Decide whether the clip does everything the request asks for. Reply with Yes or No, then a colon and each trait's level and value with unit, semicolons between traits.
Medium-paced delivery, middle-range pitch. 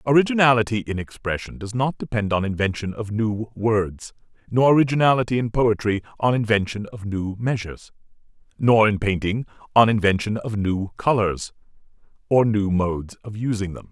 No: average, 145 wpm; low, 110 Hz